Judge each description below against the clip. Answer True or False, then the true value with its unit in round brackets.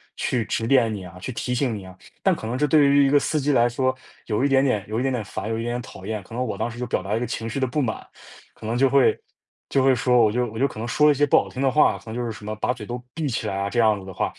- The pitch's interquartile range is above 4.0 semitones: False (3.6 semitones)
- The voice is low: True (120 Hz)